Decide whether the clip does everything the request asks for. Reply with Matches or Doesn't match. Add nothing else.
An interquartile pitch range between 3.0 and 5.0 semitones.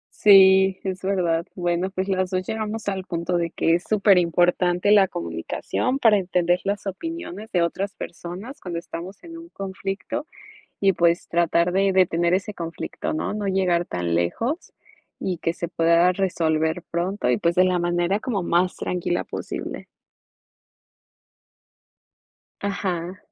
Doesn't match